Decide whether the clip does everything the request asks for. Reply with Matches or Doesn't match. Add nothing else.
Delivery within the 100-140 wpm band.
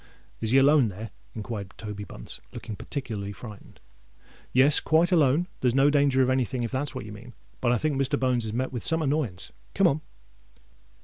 Doesn't match